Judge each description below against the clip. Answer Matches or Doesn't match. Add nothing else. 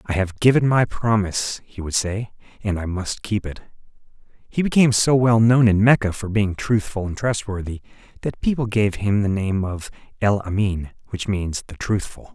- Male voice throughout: Matches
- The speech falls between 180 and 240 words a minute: Matches